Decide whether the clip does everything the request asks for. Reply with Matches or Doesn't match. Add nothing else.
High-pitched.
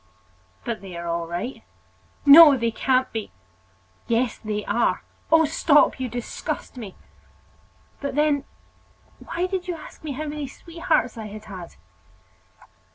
Matches